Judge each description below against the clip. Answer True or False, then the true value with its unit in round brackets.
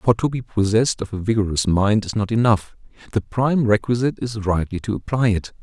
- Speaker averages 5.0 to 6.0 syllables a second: True (5.9 syllables/s)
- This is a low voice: True (110 Hz)